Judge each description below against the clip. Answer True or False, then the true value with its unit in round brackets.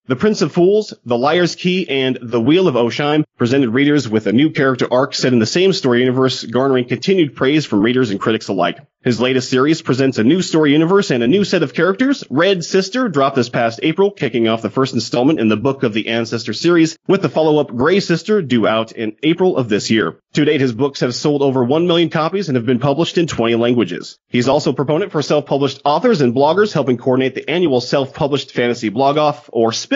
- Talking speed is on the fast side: True (230 wpm)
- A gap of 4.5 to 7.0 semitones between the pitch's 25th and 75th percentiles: True (4.9 semitones)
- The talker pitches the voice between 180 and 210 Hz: False (140 Hz)